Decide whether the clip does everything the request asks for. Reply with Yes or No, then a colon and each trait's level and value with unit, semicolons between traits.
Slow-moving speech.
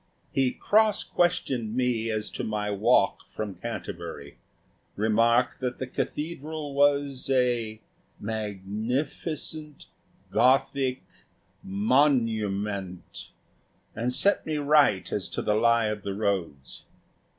Yes: slow, 105 wpm